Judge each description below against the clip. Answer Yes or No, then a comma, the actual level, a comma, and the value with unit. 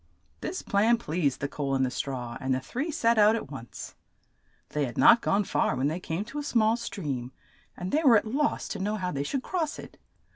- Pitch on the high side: Yes, high, 195 Hz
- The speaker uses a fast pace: Yes, fast, 225 wpm